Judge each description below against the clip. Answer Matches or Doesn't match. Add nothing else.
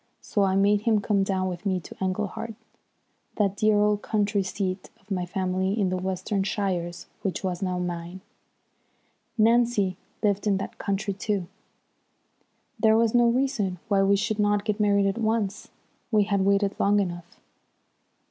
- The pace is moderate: Matches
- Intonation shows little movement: Matches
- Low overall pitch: Doesn't match